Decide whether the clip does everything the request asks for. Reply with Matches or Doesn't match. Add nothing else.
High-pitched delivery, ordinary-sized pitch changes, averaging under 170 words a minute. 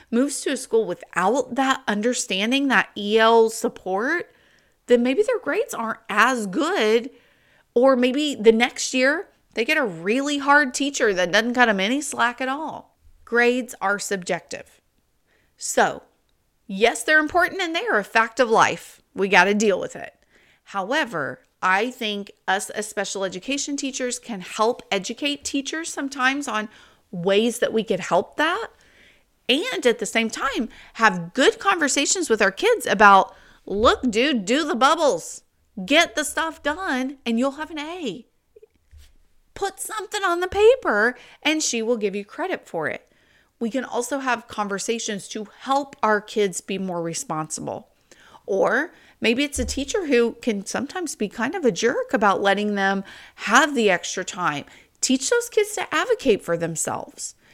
Doesn't match